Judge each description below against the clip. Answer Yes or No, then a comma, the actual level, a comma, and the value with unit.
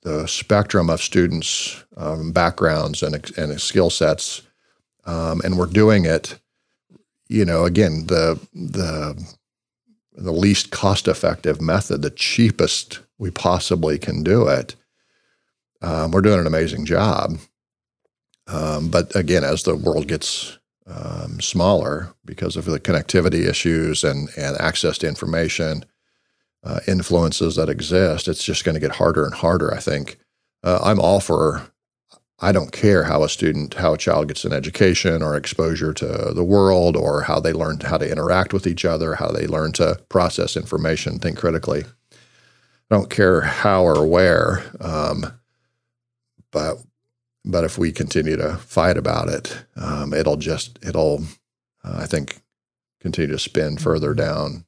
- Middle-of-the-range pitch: No, very low, 85 Hz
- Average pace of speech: Yes, average, 150 wpm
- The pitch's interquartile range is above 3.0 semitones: Yes, average, 3.4 semitones